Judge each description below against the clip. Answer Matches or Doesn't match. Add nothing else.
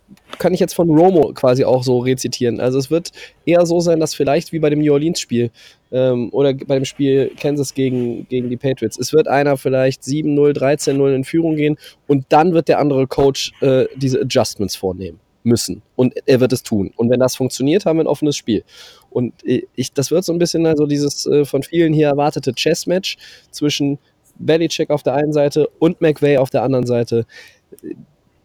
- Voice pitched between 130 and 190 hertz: Matches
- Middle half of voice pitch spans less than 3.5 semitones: Matches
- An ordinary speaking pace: Doesn't match